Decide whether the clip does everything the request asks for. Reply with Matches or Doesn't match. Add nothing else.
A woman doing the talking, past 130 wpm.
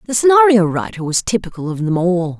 Matches